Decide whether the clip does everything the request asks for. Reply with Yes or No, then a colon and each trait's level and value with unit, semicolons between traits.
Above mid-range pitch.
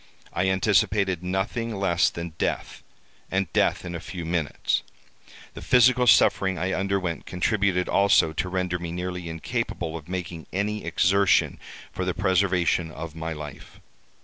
No: very low, 90 Hz